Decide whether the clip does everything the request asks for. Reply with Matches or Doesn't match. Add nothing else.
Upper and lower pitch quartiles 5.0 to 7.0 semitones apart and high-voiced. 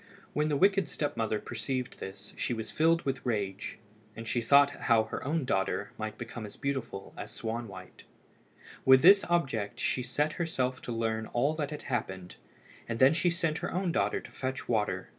Doesn't match